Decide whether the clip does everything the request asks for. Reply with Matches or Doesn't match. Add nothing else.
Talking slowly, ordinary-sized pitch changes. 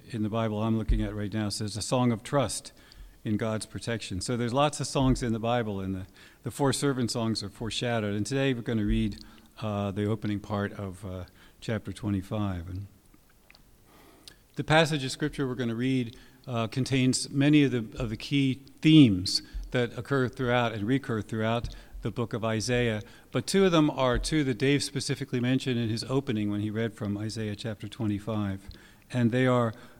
Doesn't match